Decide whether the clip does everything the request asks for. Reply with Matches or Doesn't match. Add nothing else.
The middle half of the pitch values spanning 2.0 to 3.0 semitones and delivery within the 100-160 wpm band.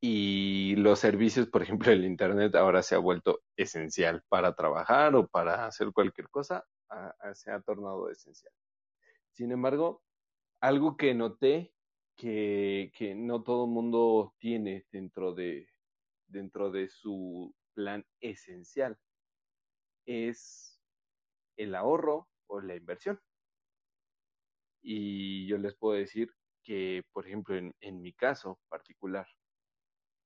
Doesn't match